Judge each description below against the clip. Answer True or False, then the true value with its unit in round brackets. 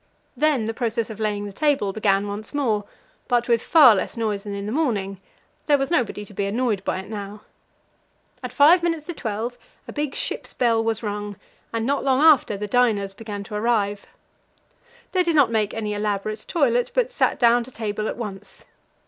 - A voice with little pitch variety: False (3.9 semitones)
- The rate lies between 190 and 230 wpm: True (195 wpm)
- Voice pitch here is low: False (225 Hz)